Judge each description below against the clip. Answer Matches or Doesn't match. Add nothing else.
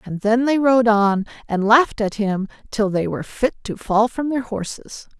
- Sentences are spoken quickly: Matches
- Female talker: Matches